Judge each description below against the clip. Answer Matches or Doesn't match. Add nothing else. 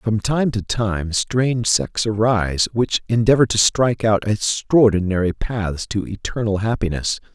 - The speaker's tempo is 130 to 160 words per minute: Matches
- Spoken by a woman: Doesn't match